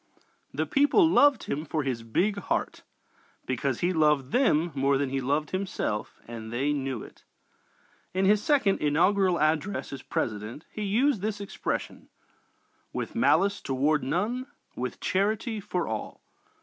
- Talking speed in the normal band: Yes, average, 145 wpm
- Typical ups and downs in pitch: No, wide, 7.0 semitones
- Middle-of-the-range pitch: Yes, medium, 165 Hz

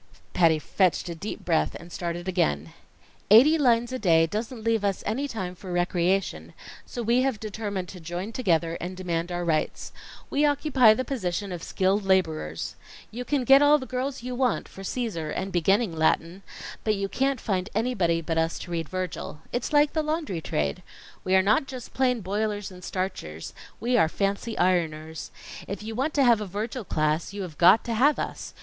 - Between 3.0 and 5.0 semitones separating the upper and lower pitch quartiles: No, wide, 5.6 semitones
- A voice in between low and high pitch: No, high, 195 Hz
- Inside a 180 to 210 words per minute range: Yes, average, 190 wpm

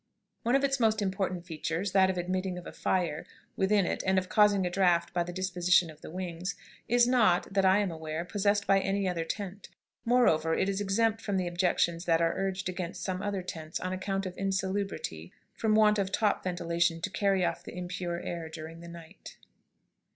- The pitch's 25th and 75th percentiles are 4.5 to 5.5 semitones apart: No, narrow, 2.5 semitones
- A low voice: No, medium, 185 Hz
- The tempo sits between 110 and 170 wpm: No, average, 200 wpm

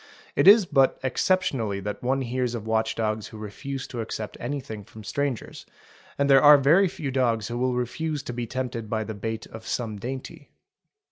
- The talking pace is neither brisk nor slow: Yes, average, 190 wpm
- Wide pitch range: No, average, 3.7 semitones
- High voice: No, low, 125 Hz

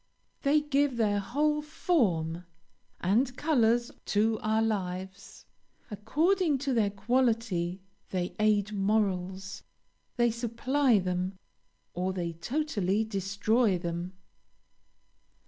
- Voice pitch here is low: No, high, 215 Hz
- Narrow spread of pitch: No, average, 5.0 semitones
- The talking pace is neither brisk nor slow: No, slow, 95 wpm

